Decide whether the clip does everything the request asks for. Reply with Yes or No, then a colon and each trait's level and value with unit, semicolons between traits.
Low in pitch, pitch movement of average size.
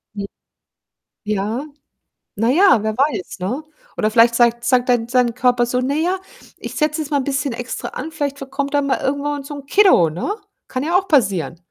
No: very high, 260 Hz; average, 3.8 semitones